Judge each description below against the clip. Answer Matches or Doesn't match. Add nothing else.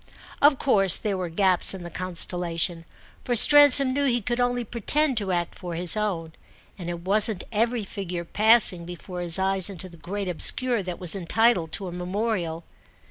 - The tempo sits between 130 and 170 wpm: Doesn't match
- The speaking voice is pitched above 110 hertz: Matches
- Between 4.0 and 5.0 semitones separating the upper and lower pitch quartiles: Matches